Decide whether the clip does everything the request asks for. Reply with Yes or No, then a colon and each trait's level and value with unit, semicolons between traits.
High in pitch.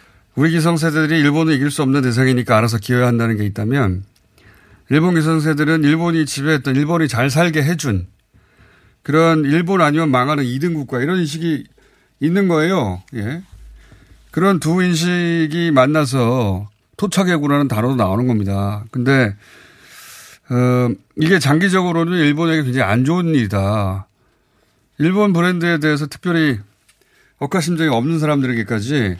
No: medium, 140 Hz